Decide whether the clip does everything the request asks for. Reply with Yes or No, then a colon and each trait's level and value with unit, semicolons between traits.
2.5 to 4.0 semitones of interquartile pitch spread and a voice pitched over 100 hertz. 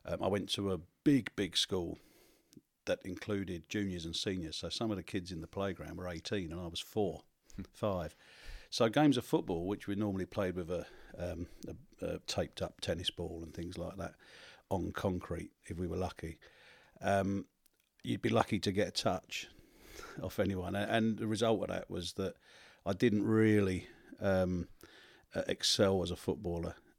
No: average, 2.8 semitones; very low, 95 Hz